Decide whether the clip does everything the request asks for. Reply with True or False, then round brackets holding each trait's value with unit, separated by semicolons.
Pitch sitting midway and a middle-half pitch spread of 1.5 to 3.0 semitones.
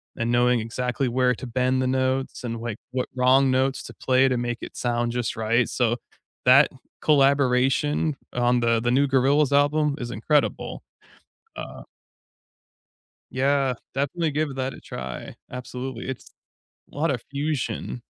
False (130 Hz; 2.4 semitones)